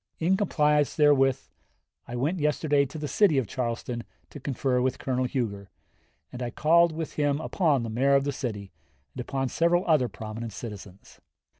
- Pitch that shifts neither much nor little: Yes, average, 3.9 semitones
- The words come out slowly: No, average, 170 wpm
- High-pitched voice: No, low, 135 Hz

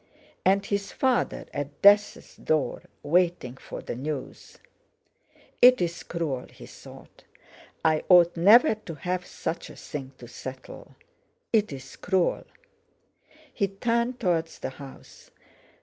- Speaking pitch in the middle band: Yes, medium, 175 Hz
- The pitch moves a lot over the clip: Yes, wide, 5.7 semitones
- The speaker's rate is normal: No, slow, 115 wpm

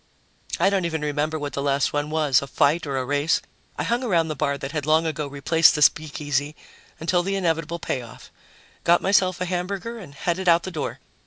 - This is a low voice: No, medium, 155 Hz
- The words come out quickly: Yes, fast, 210 wpm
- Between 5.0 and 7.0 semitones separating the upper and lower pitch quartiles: No, average, 3.4 semitones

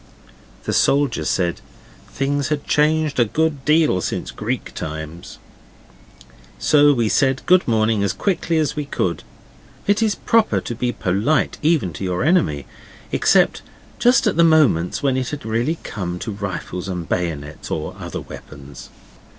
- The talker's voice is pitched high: No, low, 125 Hz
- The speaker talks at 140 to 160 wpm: Yes, average, 150 wpm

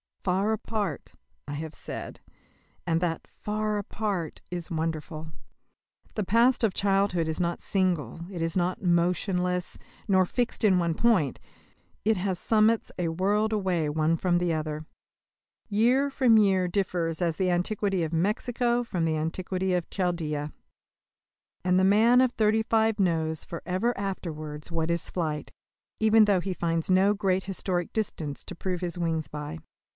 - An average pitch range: Yes, average, 3.9 semitones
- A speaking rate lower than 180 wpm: Yes, average, 150 wpm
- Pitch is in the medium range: Yes, medium, 180 Hz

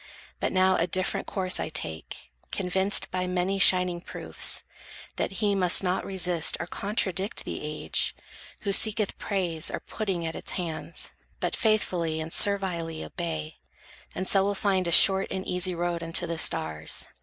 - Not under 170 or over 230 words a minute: No, average, 160 wpm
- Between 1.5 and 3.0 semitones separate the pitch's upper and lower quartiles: Yes, average, 2.7 semitones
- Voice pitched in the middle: Yes, medium, 180 Hz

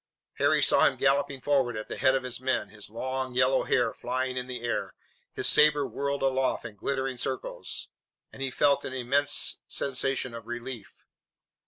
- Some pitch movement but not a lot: No, narrow, 1.9 semitones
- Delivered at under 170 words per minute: No, average, 175 wpm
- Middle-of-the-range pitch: No, low, 130 Hz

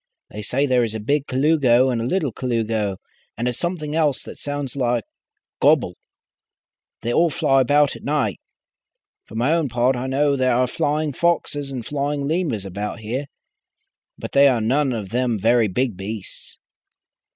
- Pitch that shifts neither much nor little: Yes, average, 3.8 semitones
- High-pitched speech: No, low, 130 Hz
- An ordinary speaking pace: Yes, average, 170 wpm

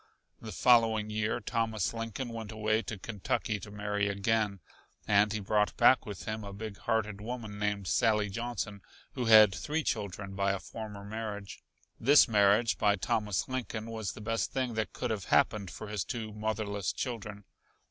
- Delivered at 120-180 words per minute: Yes, average, 170 wpm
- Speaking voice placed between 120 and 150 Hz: No, low, 110 Hz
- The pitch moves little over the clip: Yes, narrow, 1.8 semitones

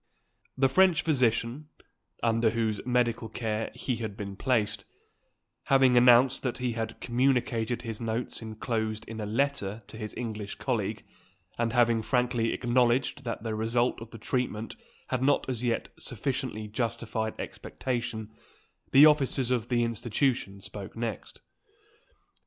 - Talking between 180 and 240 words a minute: No, slow, 135 wpm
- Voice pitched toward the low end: Yes, low, 120 Hz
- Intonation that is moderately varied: No, narrow, 2.3 semitones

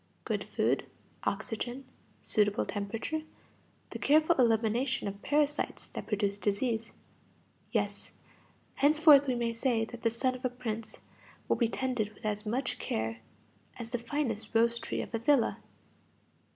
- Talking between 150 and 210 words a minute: No, average, 140 wpm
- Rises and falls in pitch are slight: No, average, 3.2 semitones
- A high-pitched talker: Yes, high, 235 Hz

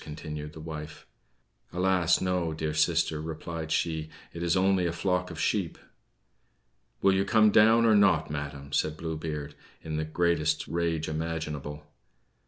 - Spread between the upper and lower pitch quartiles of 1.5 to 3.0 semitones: Yes, average, 2.7 semitones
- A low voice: Yes, very low, 80 Hz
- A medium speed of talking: Yes, average, 150 wpm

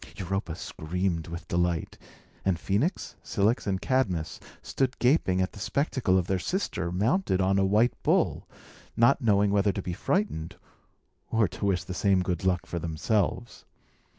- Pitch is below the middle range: Yes, very low, 95 Hz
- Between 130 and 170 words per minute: Yes, average, 155 wpm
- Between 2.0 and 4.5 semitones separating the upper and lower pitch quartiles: Yes, average, 3.8 semitones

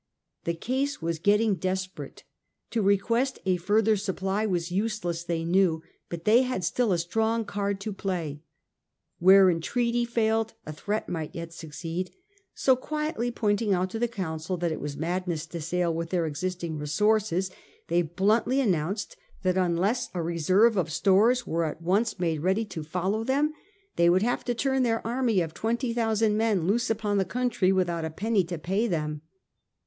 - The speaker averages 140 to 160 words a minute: No, average, 175 wpm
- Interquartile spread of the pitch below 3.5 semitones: No, average, 4.8 semitones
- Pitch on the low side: No, high, 190 Hz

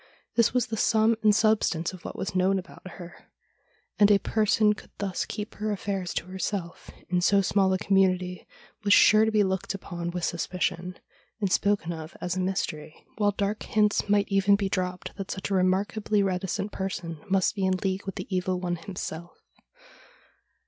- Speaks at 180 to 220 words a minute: Yes, average, 185 wpm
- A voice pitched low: No, high, 190 Hz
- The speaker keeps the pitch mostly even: Yes, narrow, 2.2 semitones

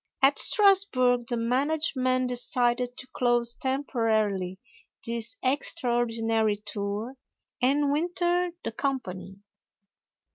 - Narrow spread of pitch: No, average, 3.6 semitones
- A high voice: Yes, high, 245 Hz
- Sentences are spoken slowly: Yes, slow, 85 wpm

